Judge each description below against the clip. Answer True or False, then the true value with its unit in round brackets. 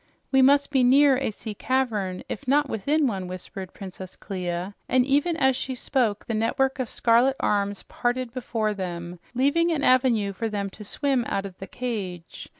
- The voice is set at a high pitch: True (235 Hz)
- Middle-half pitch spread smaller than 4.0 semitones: False (5.2 semitones)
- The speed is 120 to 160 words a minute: False (180 wpm)